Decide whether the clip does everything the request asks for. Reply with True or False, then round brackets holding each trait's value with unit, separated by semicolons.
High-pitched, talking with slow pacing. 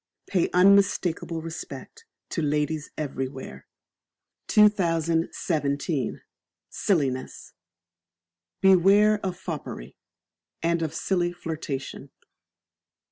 False (165 Hz; 70 wpm)